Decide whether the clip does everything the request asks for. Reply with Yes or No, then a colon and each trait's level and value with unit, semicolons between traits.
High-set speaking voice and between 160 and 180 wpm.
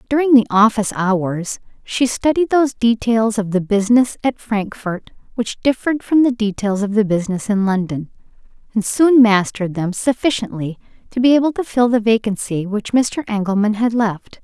Yes: high, 220 Hz; average, 165 wpm